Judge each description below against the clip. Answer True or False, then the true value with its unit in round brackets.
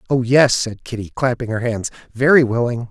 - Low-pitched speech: True (120 Hz)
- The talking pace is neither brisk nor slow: True (185 wpm)